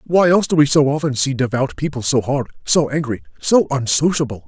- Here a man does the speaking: Yes, male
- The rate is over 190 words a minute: Yes, average, 200 wpm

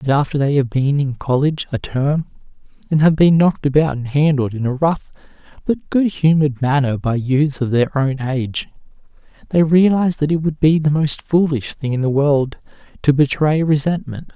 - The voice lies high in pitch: No, medium, 145 Hz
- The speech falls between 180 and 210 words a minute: Yes, average, 190 wpm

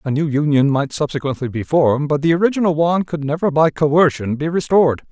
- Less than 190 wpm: No, average, 200 wpm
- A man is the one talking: Yes, male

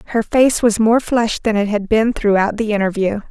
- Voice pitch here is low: No, high, 215 Hz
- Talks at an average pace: No, fast, 220 wpm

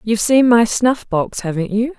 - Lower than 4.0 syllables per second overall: No, 4.8 syllables/s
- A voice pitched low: No, high, 220 Hz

